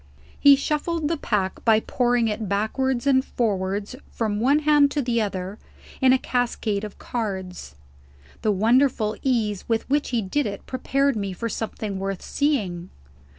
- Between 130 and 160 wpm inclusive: Yes, average, 155 wpm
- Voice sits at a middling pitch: No, high, 225 Hz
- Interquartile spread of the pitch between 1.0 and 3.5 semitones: No, average, 4.7 semitones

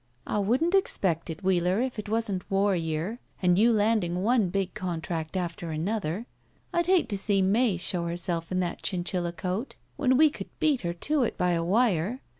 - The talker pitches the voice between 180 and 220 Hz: Yes, high, 190 Hz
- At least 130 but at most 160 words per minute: No, average, 190 wpm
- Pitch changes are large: No, average, 4.7 semitones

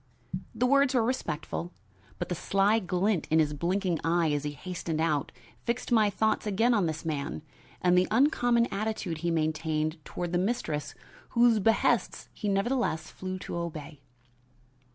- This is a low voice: No, medium, 180 Hz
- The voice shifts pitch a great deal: Yes, wide, 5.7 semitones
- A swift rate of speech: No, average, 155 wpm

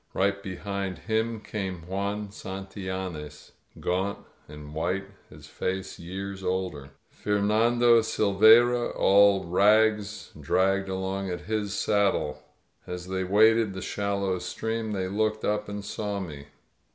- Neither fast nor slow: No, slow, 120 wpm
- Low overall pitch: Yes, low, 100 Hz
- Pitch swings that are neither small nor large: No, narrow, 2.1 semitones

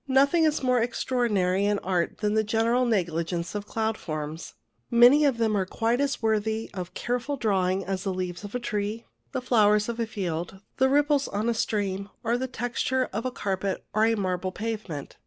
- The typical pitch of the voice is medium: No, high, 215 Hz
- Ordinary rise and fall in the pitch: Yes, average, 4.2 semitones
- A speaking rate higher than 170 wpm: Yes, average, 195 wpm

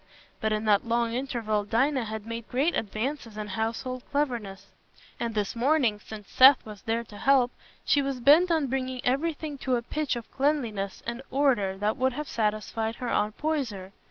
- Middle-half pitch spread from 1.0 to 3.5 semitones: No, average, 4.1 semitones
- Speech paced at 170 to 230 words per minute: Yes, average, 180 wpm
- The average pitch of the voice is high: Yes, high, 235 Hz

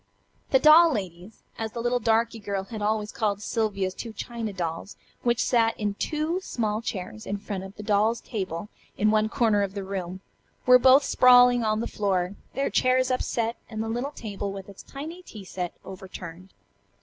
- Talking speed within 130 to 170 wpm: No, average, 185 wpm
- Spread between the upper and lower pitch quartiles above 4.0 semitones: No, average, 3.5 semitones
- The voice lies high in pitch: Yes, high, 215 Hz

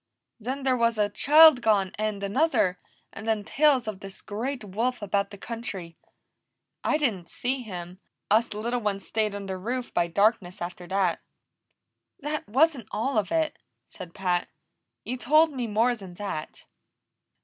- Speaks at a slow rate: No, average, 155 wpm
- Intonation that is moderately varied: Yes, average, 4.5 semitones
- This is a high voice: Yes, high, 215 Hz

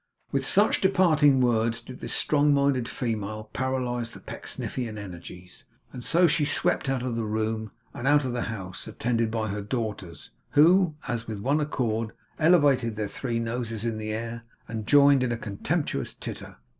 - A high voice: No, low, 120 Hz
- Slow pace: No, average, 170 wpm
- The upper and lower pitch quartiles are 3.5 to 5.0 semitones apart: Yes, average, 4.1 semitones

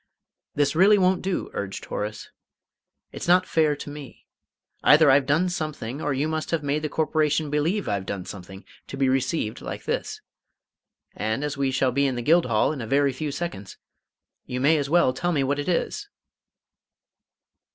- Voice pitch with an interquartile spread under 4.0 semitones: Yes, average, 3.5 semitones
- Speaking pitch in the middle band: Yes, medium, 145 Hz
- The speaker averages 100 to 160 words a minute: No, average, 180 wpm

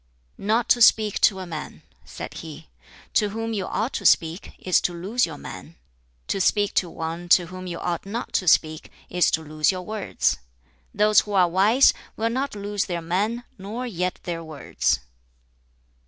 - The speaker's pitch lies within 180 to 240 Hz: Yes, medium, 185 Hz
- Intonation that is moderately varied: Yes, average, 3.9 semitones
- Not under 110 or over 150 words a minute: No, average, 180 wpm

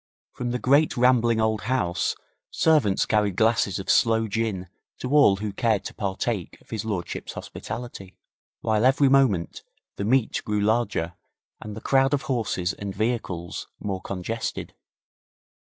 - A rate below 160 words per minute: Yes, average, 145 wpm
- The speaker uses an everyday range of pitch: Yes, average, 3.9 semitones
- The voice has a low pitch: Yes, low, 110 Hz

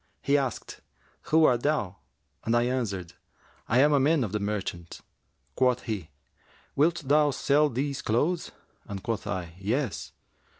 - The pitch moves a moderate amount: No, wide, 5.8 semitones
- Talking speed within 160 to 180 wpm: No, average, 145 wpm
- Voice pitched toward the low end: Yes, low, 125 Hz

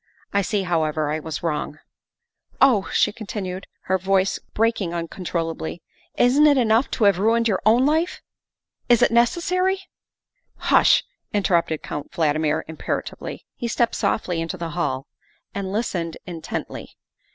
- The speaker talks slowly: No, average, 160 wpm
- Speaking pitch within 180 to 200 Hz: Yes, high, 190 Hz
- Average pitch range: No, wide, 5.8 semitones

